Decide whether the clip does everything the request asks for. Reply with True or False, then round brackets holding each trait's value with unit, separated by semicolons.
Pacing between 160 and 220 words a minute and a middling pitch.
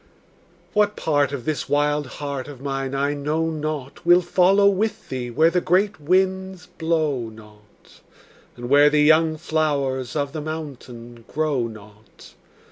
False (145 wpm; 150 Hz)